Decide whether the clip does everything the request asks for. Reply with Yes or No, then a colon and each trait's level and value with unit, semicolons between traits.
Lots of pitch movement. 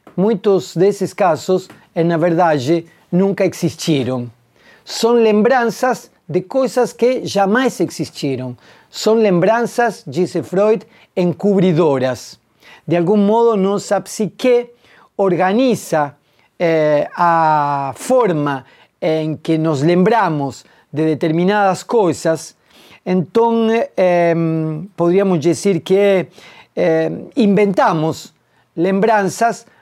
No: average, 4.8 semitones